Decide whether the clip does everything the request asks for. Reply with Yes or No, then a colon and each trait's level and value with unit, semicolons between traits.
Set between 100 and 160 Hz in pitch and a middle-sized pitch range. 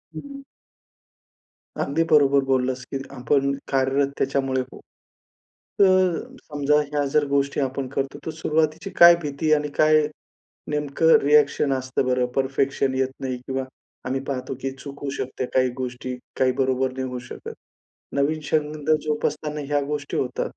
No: medium, 140 Hz; narrow, 2.2 semitones